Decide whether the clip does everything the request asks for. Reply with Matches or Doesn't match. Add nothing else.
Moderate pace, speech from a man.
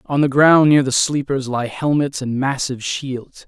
Matches